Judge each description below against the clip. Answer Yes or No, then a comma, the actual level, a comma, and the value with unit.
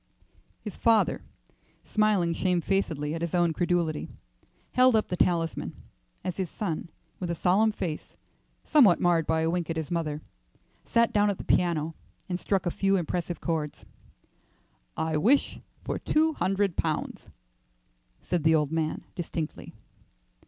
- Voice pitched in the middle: Yes, medium, 175 Hz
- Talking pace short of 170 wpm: Yes, average, 145 wpm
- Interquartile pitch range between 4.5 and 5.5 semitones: No, average, 3.4 semitones